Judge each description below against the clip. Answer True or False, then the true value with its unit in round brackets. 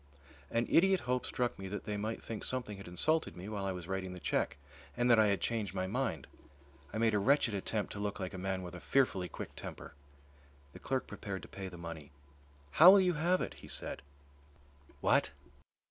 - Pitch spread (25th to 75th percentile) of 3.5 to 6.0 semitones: True (4.8 semitones)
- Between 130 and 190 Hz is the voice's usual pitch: False (105 Hz)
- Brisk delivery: True (210 wpm)